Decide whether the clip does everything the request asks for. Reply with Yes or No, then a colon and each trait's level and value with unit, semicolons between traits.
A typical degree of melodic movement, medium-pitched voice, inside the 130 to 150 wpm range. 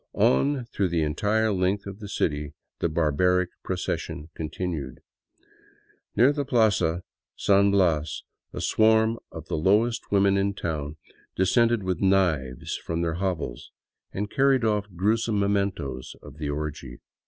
No: average, 5.0 semitones; very low, 95 Hz; slow, 135 wpm